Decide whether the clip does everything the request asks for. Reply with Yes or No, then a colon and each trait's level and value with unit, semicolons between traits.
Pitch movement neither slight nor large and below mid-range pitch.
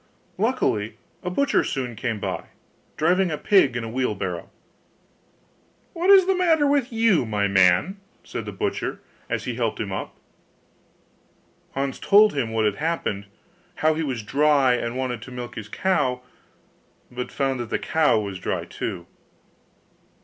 No: wide, 8.1 semitones; low, 130 Hz